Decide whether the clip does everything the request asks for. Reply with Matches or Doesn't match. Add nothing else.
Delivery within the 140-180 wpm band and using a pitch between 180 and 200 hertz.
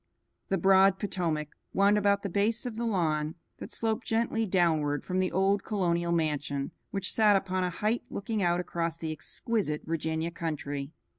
Matches